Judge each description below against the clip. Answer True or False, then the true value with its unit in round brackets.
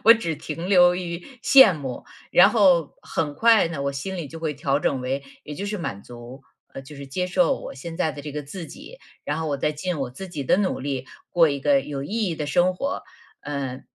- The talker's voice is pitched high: False (150 Hz)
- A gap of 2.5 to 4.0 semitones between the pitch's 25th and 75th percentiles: False (4.5 semitones)